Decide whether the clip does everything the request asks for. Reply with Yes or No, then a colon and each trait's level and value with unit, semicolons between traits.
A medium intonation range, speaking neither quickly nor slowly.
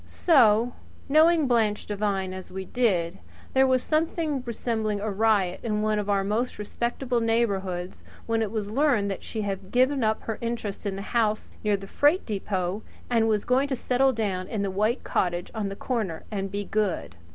Yes: average, 3.6 semitones; average, 185 wpm